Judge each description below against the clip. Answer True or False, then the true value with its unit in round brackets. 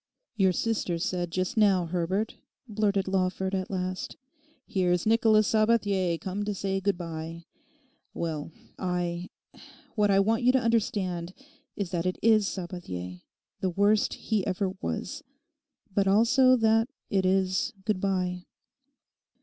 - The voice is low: False (190 Hz)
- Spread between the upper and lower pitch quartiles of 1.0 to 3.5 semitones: True (3.0 semitones)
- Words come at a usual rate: False (130 wpm)